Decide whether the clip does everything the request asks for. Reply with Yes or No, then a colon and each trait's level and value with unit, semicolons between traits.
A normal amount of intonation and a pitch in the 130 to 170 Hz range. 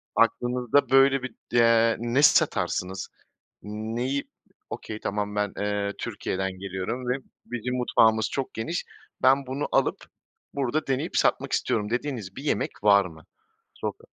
No: average, 4.0 semitones; low, 115 Hz